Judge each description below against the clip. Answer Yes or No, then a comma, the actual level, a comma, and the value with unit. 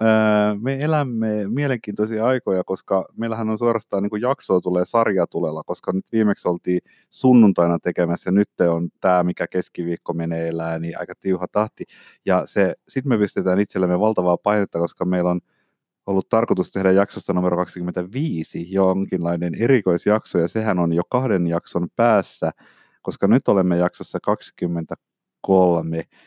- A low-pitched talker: Yes, very low, 95 Hz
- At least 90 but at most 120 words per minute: No, average, 135 wpm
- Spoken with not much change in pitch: No, average, 3.3 semitones